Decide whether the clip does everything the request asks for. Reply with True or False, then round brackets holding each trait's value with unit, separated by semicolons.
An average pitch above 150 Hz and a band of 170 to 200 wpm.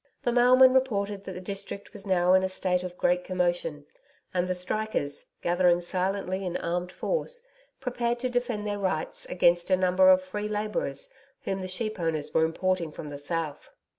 True (185 Hz; 180 wpm)